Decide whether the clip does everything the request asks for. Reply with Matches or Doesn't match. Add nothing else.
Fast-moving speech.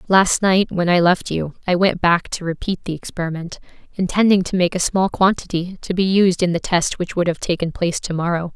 Matches